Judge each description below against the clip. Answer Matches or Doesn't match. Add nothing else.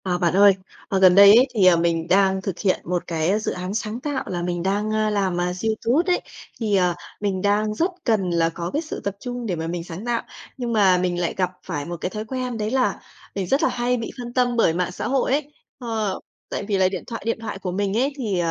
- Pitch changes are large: Doesn't match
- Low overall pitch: Doesn't match